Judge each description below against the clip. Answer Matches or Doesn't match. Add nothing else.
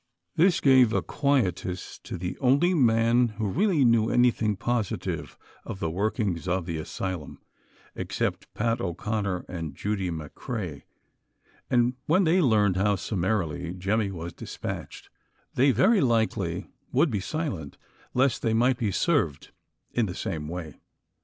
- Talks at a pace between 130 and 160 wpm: Matches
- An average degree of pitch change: Doesn't match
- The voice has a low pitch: Matches